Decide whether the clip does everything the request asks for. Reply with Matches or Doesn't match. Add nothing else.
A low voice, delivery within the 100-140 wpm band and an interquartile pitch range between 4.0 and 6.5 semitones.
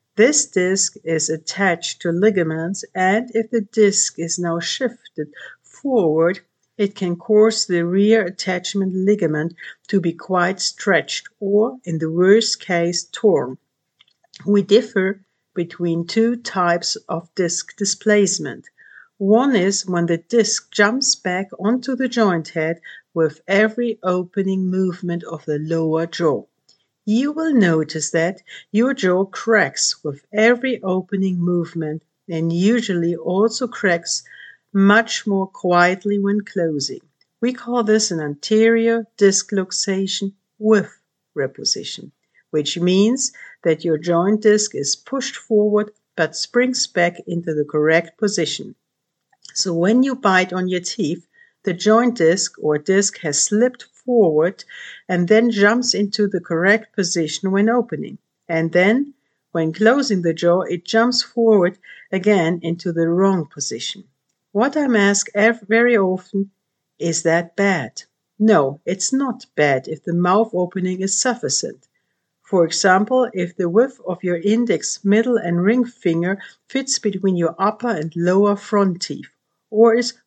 Doesn't match